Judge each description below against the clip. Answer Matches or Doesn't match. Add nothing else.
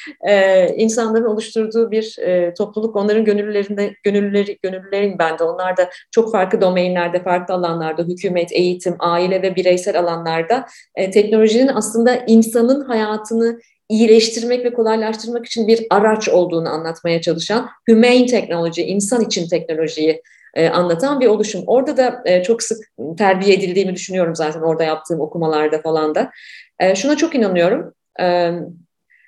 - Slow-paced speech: Doesn't match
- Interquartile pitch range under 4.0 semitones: Doesn't match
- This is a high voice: Matches